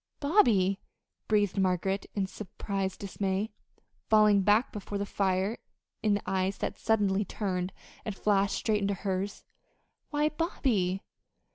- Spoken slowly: Yes, slow, 125 wpm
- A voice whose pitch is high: Yes, high, 200 Hz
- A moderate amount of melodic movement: No, narrow, 1.8 semitones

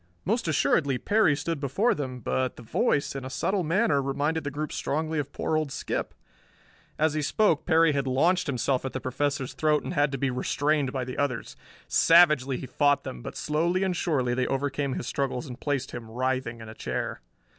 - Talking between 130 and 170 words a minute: No, average, 200 wpm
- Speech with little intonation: No, average, 3.2 semitones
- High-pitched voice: No, medium, 145 Hz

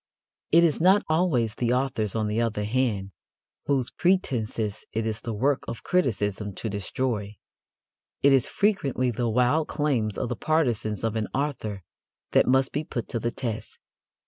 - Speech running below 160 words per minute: No, average, 165 wpm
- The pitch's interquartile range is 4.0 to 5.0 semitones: Yes, average, 4.6 semitones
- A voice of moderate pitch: No, low, 120 Hz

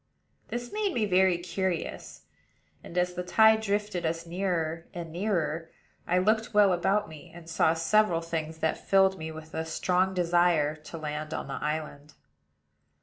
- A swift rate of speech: No, average, 160 wpm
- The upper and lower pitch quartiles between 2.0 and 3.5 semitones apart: Yes, average, 3.1 semitones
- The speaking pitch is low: No, medium, 175 Hz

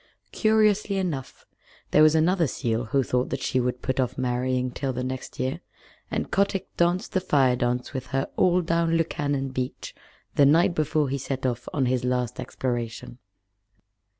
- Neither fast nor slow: Yes, average, 170 wpm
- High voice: No, low, 135 Hz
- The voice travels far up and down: No, average, 4.7 semitones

